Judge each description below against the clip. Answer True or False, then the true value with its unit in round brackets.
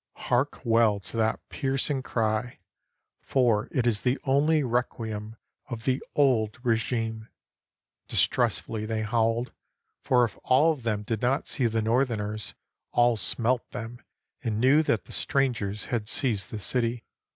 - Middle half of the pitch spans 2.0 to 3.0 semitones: True (2.7 semitones)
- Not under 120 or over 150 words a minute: True (140 wpm)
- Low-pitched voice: True (115 Hz)